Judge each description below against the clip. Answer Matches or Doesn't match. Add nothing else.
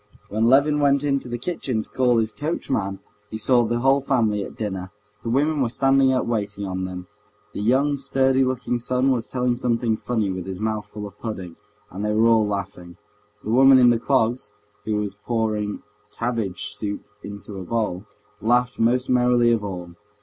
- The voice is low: Matches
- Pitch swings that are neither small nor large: Matches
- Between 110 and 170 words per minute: Doesn't match